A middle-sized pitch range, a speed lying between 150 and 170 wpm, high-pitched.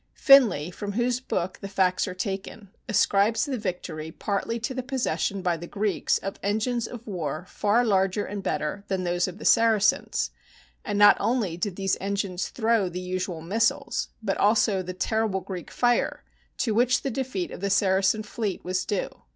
No: average, 3.5 semitones; average, 180 wpm; high, 200 Hz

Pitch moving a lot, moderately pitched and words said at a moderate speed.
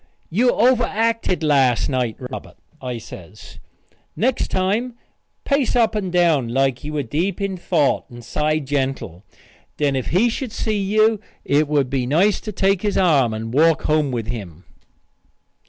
Yes: wide, 7.8 semitones; medium, 155 Hz; average, 155 wpm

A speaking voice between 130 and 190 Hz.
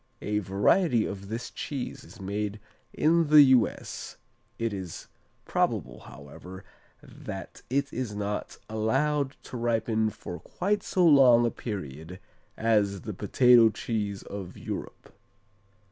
No: low, 110 Hz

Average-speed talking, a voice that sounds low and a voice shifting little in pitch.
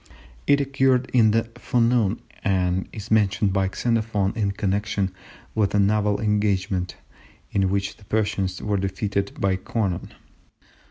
No: slow, 130 wpm; low, 100 Hz; narrow, 2.2 semitones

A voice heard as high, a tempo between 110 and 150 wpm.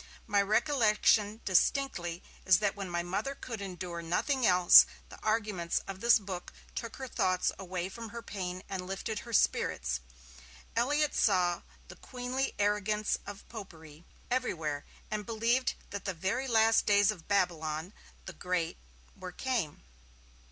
Yes: high, 200 Hz; average, 145 wpm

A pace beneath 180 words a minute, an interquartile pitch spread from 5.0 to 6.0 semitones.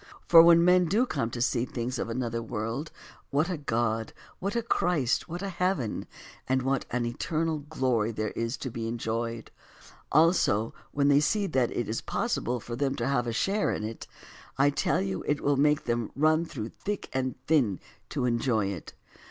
No: average, 195 wpm; average, 5.3 semitones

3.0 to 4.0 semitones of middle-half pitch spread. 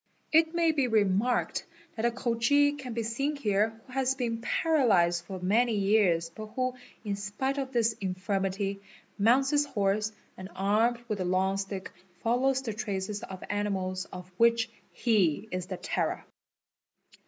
No: average, 4.5 semitones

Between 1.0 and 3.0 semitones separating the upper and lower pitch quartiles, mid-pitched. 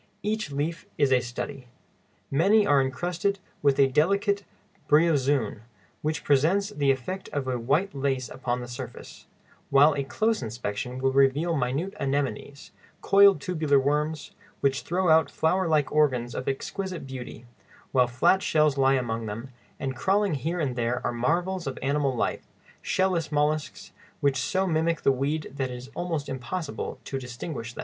No: average, 4.2 semitones; medium, 145 Hz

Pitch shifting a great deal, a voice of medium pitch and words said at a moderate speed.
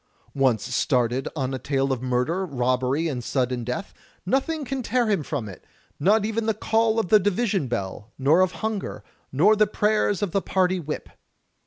Yes: wide, 8.7 semitones; medium, 170 Hz; average, 180 wpm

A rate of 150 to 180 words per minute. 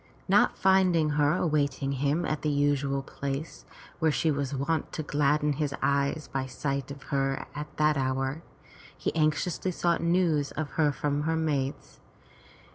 Yes: average, 155 wpm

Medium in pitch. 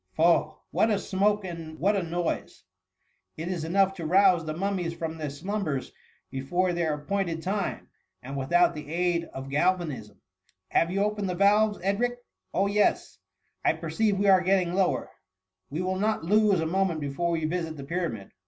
Yes: medium, 175 Hz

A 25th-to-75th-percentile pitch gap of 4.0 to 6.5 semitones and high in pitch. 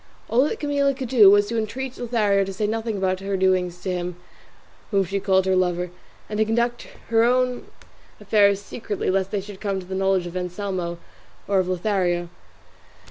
No: average, 3.2 semitones; high, 200 Hz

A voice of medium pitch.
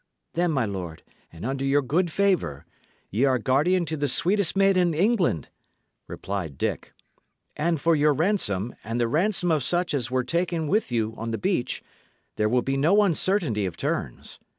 Yes: medium, 145 Hz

